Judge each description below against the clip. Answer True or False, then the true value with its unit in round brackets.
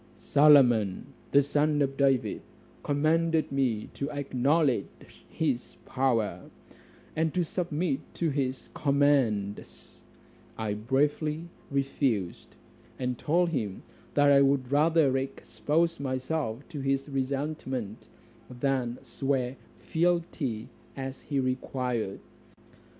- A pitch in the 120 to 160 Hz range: True (135 Hz)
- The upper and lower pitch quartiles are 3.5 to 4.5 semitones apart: False (2.9 semitones)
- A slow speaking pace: True (95 wpm)